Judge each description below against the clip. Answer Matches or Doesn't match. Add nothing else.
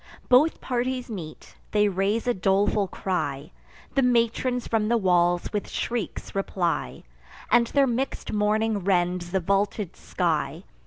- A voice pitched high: Matches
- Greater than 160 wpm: Doesn't match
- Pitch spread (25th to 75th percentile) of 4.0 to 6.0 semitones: Matches